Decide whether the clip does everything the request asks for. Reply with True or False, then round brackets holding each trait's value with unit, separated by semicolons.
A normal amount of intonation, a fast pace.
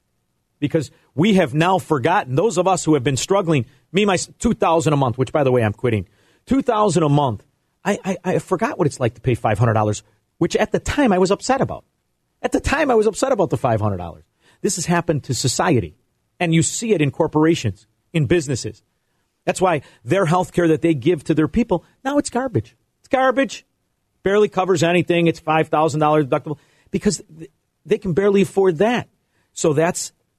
False (6.2 semitones; 210 wpm)